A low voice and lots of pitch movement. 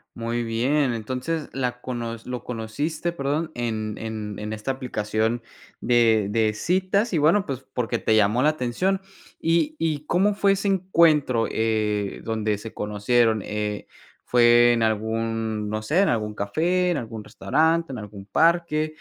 Yes: low, 120 Hz; wide, 6.1 semitones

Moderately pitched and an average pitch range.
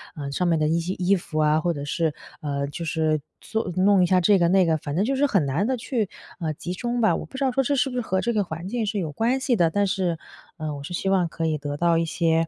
Yes: medium, 175 Hz; average, 4.7 semitones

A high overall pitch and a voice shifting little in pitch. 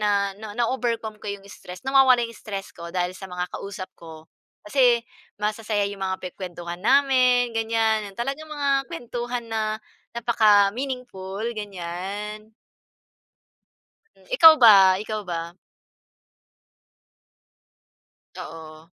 No: high, 215 Hz; average, 4.2 semitones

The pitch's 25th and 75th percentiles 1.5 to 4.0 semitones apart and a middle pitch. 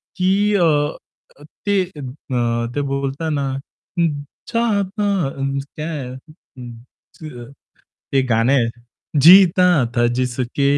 No: average, 5.3 semitones; medium, 145 Hz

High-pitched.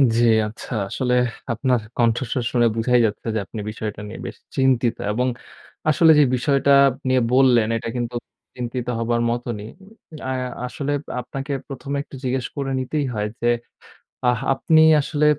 No: low, 125 Hz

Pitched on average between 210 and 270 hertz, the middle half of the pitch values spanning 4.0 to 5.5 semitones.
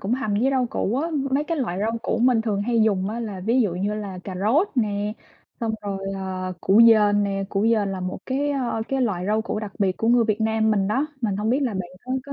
No: high, 215 Hz; average, 3.3 semitones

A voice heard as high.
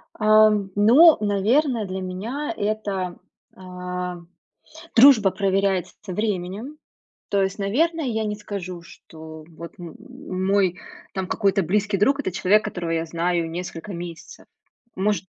Yes: high, 195 Hz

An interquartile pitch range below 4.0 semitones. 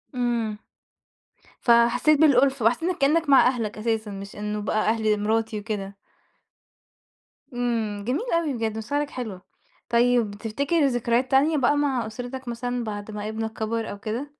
Yes: average, 3.6 semitones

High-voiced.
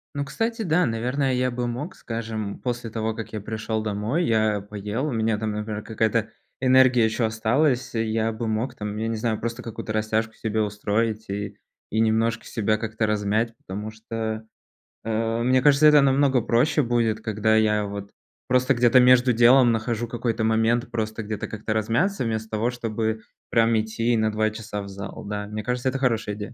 No: low, 110 Hz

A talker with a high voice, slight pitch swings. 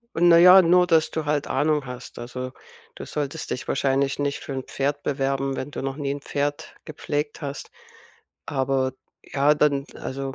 No: medium, 140 Hz; narrow, 1.8 semitones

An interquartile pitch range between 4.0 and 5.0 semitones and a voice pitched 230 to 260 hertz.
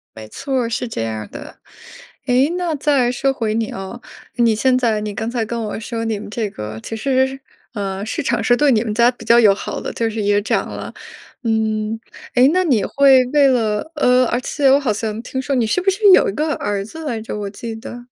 No: average, 3.6 semitones; high, 235 Hz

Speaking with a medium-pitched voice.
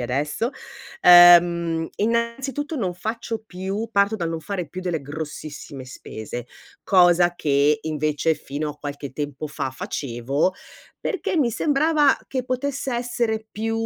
Yes: medium, 175 Hz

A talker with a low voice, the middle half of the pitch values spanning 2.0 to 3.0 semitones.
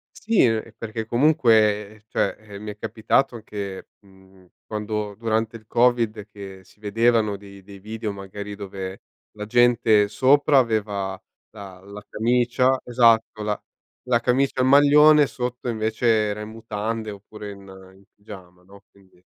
Yes: low, 110 Hz; narrow, 2.6 semitones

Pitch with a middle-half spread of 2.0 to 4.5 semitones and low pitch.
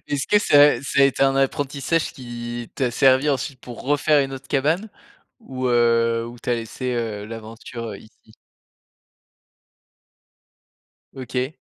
Yes: average, 2.9 semitones; low, 130 Hz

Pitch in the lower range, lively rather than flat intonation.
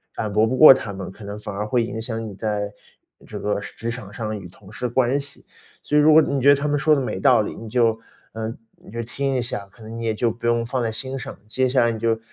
No: low, 115 Hz; average, 3.2 semitones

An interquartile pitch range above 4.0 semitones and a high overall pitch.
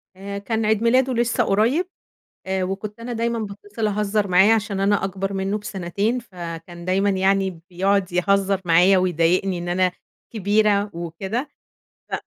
No: narrow, 2.5 semitones; high, 200 Hz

